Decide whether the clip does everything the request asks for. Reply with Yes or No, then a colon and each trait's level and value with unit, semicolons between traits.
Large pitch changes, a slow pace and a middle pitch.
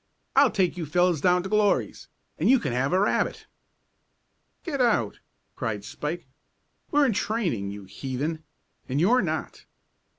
No: wide, 8.0 semitones; average, 145 wpm; medium, 175 Hz